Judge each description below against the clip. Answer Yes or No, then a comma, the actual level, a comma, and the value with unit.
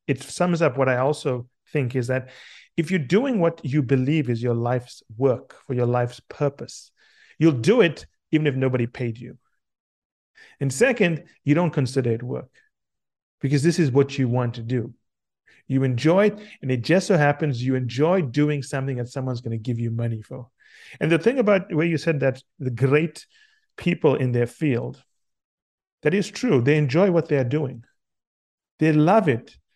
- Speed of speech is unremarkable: Yes, average, 185 wpm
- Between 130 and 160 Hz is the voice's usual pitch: Yes, medium, 140 Hz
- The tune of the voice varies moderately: Yes, average, 4.7 semitones